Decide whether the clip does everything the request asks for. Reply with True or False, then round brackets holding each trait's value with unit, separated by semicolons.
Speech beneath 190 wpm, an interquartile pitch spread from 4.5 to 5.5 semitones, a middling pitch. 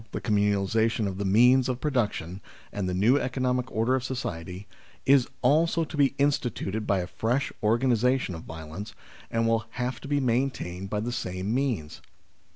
False (165 wpm; 4.8 semitones; 115 Hz)